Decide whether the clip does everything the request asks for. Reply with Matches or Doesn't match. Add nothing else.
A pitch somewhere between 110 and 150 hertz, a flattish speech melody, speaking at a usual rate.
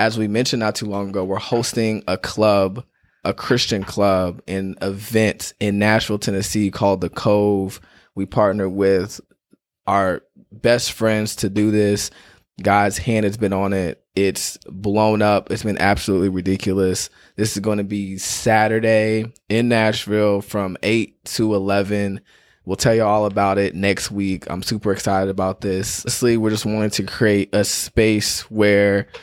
Doesn't match